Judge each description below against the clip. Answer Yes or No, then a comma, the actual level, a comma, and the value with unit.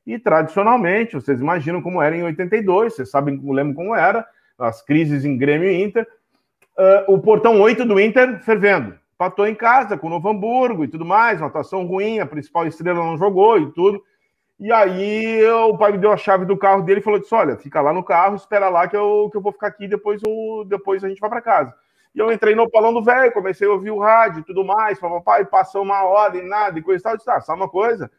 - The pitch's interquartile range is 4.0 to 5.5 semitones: No, average, 3.6 semitones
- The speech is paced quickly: Yes, fast, 230 wpm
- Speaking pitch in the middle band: No, high, 200 Hz